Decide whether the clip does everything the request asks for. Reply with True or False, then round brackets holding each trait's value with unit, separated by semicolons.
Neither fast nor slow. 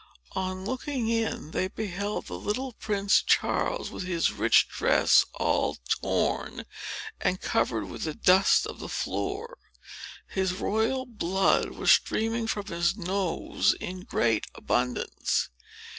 False (130 wpm)